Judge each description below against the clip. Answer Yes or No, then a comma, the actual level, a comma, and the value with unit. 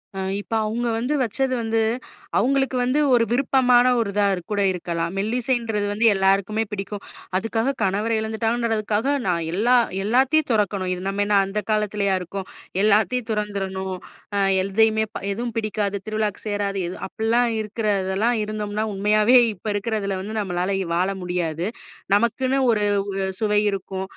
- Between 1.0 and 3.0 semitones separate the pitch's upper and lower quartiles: Yes, average, 2.7 semitones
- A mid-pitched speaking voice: No, high, 210 Hz